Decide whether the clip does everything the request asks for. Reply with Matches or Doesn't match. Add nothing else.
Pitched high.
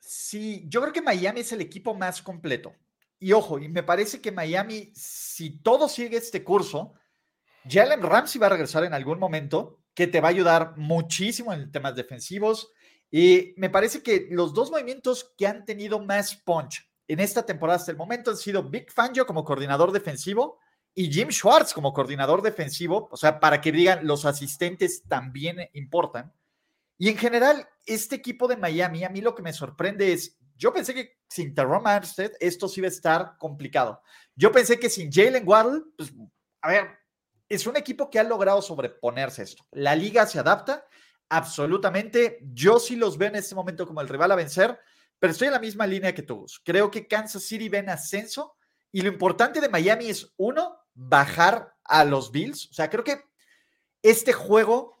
Matches